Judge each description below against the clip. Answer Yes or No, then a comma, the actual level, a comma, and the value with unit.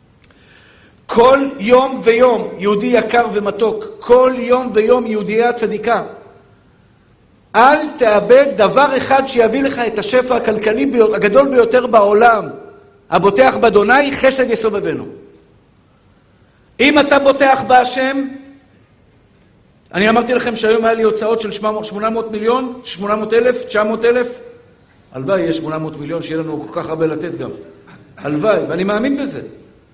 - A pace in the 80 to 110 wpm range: No, average, 120 wpm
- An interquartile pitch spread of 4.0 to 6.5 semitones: No, average, 3.4 semitones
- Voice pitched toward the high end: Yes, high, 225 Hz